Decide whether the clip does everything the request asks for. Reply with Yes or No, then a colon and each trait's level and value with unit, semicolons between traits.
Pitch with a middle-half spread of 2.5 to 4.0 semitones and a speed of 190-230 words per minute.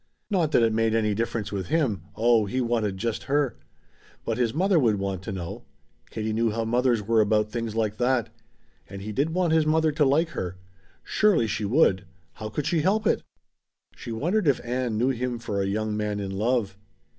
No: average, 4.6 semitones; fast, 205 wpm